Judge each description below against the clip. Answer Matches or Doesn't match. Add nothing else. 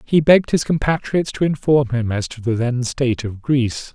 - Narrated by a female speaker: Doesn't match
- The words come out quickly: Matches